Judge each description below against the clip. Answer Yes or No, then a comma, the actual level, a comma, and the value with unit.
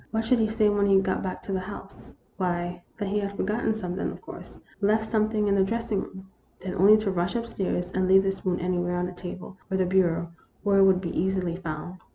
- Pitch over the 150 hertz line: Yes, high, 190 Hz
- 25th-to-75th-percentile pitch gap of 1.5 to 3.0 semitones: Yes, narrow, 2.4 semitones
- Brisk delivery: Yes, fast, 240 wpm